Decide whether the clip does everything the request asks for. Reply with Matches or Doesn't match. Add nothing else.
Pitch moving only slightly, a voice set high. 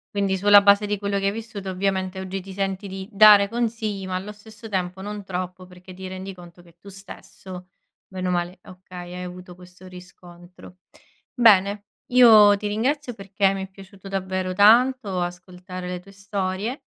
Matches